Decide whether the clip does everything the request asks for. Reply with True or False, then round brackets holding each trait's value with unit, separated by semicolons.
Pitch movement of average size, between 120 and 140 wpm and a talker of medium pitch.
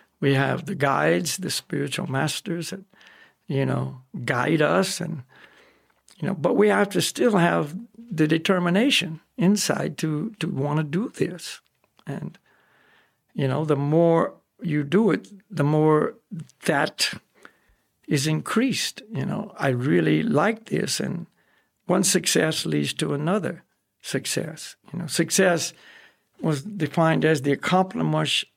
True (4.1 semitones; 135 wpm; 165 Hz)